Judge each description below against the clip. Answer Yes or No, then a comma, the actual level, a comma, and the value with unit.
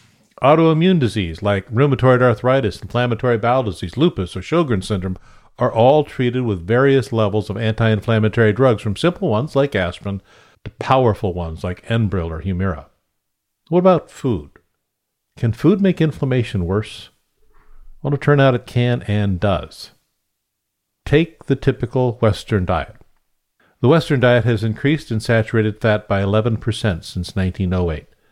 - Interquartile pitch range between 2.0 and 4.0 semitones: No, average, 4.4 semitones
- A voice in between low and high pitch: No, low, 110 Hz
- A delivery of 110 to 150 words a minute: Yes, average, 140 wpm